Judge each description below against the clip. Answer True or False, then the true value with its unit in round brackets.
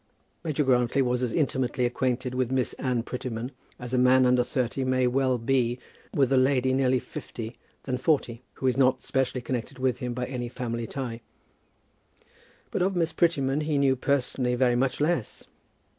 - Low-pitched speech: True (130 Hz)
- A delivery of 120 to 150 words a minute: False (175 wpm)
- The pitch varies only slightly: True (1.5 semitones)